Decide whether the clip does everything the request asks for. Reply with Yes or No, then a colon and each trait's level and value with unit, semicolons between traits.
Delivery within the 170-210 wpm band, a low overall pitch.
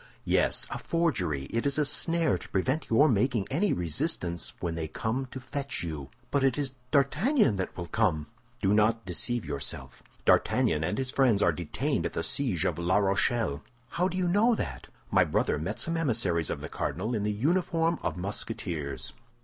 Yes: average, 185 wpm; low, 115 Hz